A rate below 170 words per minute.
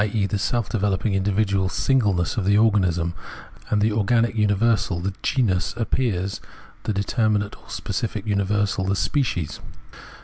Yes: average, 140 wpm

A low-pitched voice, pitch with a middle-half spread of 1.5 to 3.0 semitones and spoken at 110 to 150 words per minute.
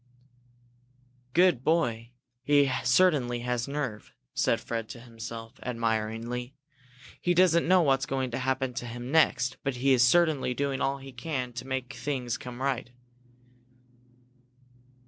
Yes: low, 130 Hz; narrow, 2.6 semitones; slow, 135 wpm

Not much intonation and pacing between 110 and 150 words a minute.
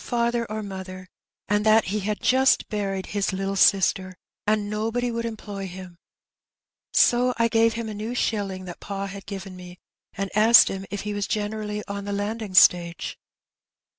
No: narrow, 2.3 semitones; average, 170 wpm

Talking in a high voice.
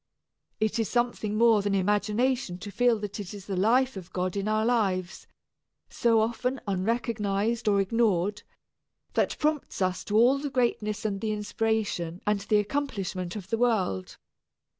Yes: high, 210 Hz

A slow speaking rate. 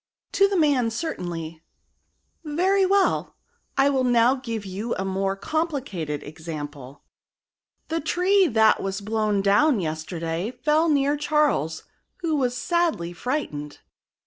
Yes: slow, 125 wpm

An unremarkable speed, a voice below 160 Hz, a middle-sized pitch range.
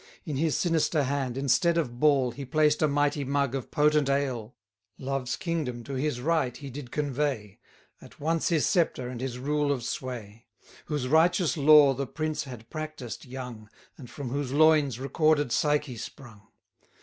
Yes: average, 170 wpm; medium, 140 Hz; average, 3.2 semitones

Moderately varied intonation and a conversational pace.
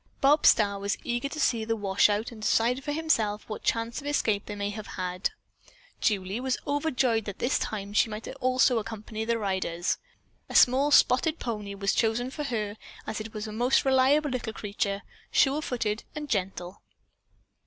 Yes: average, 4.0 semitones; average, 175 wpm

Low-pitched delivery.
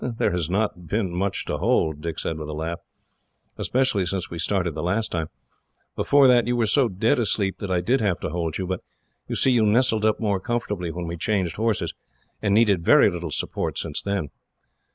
Yes: very low, 95 Hz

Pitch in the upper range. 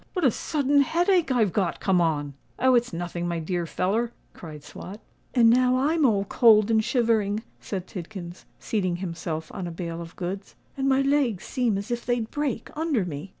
Yes: high, 215 Hz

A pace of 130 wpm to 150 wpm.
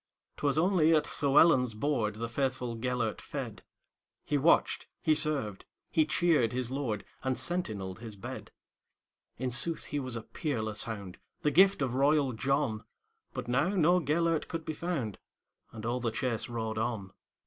Yes: slow, 135 wpm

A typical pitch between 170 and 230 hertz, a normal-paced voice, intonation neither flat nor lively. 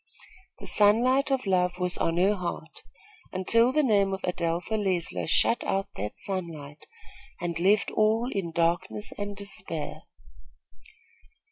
No: high, 190 Hz; slow, 130 wpm; average, 3.5 semitones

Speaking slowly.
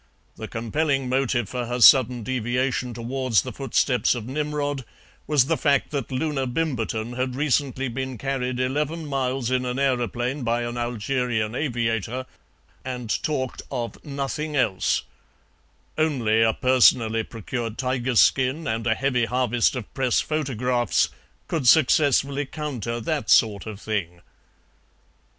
Yes: slow, 130 wpm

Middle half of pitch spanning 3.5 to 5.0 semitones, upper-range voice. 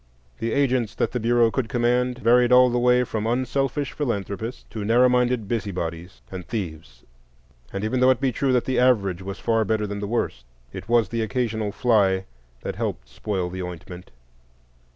No: average, 4.0 semitones; low, 115 Hz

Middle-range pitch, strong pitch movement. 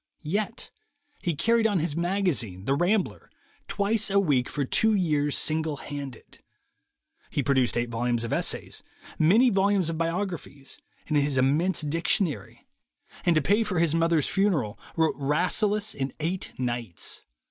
Yes: medium, 160 Hz; wide, 5.8 semitones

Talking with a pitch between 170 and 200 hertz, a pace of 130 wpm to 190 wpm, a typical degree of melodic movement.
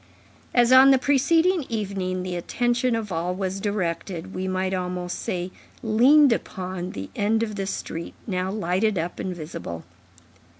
Yes: high, 190 Hz; average, 155 wpm; average, 4.1 semitones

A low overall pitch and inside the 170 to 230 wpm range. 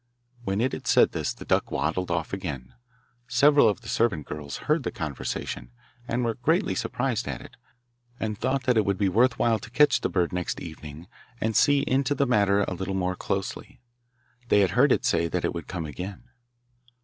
Yes: low, 100 Hz; average, 200 wpm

